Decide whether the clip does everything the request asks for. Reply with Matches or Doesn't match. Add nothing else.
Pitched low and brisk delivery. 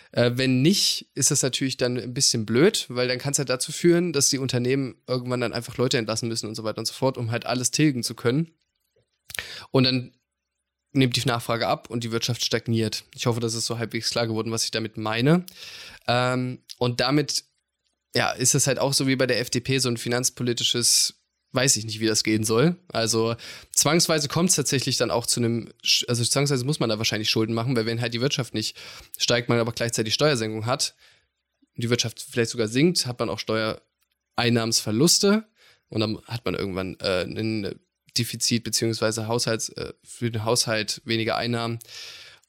Matches